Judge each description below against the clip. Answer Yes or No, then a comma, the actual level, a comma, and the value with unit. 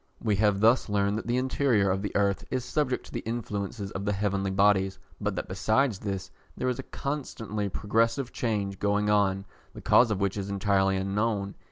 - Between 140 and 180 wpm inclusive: No, average, 195 wpm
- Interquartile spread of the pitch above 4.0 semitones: No, average, 2.7 semitones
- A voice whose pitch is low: Yes, low, 105 Hz